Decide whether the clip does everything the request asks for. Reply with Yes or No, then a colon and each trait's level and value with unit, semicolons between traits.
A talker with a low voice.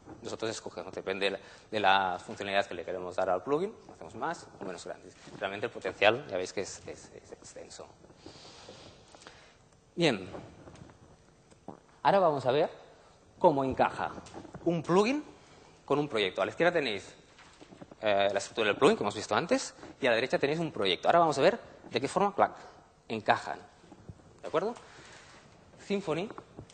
Yes: low, 130 Hz